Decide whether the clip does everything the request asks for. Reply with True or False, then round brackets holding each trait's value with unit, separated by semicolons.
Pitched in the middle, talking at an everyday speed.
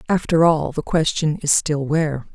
True (155 Hz; 180 wpm)